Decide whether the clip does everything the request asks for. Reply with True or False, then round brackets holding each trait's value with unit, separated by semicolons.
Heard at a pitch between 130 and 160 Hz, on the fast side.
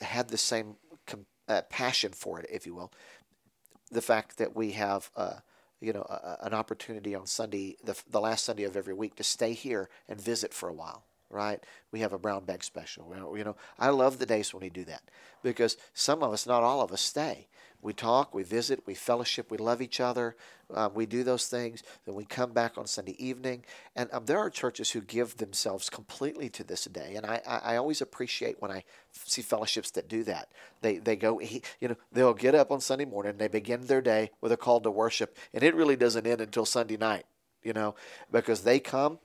False (115 Hz; 220 wpm)